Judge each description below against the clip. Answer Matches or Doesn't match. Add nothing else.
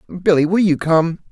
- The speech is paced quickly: Doesn't match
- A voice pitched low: Doesn't match